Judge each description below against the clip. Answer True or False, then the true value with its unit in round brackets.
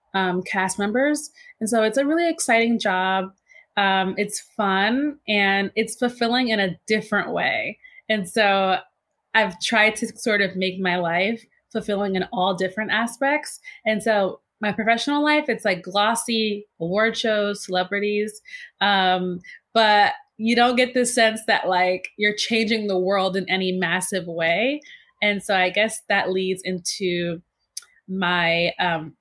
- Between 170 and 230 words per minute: False (150 wpm)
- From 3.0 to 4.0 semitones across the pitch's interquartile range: True (3.4 semitones)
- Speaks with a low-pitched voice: False (210 Hz)